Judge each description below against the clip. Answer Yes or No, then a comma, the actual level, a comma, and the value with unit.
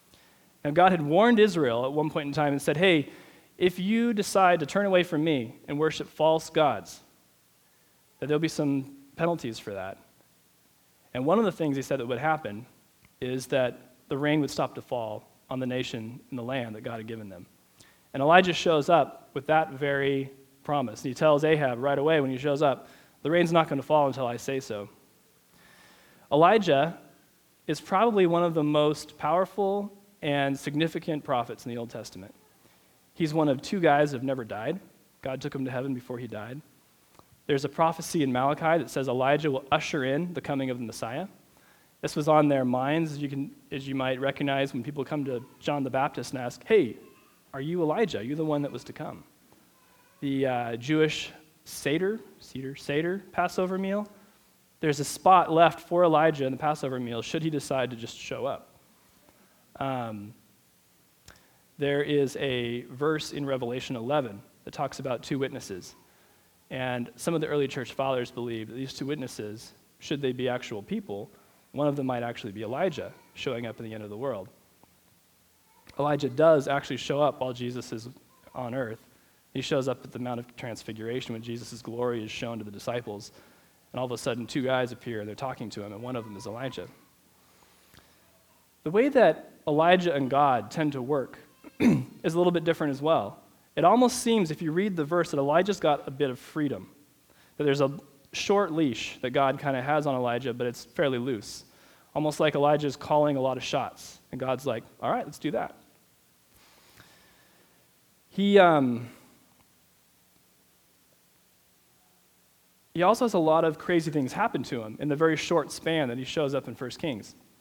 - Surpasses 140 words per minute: Yes, average, 190 wpm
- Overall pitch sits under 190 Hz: Yes, medium, 140 Hz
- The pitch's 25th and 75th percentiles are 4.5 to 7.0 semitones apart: No, average, 4.1 semitones